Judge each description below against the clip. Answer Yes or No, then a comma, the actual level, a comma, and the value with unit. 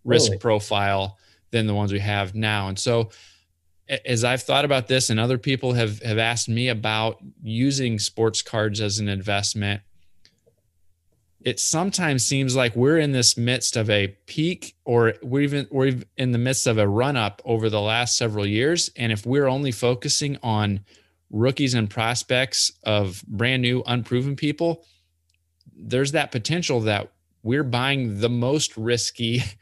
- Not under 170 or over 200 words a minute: No, average, 160 wpm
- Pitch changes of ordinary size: Yes, average, 3.8 semitones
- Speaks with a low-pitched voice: Yes, low, 115 Hz